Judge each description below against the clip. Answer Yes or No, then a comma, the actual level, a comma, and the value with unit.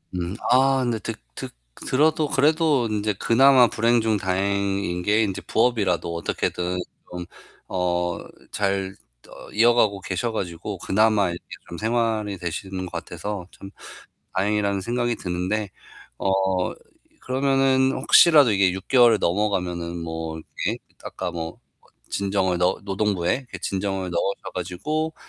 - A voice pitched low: Yes, low, 100 Hz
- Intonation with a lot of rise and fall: No, average, 4.6 semitones